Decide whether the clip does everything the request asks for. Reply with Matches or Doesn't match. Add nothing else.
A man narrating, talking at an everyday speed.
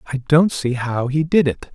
Doesn't match